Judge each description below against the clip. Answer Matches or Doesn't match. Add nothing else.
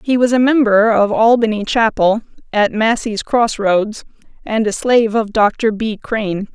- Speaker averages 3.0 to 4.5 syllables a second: Matches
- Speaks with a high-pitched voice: Matches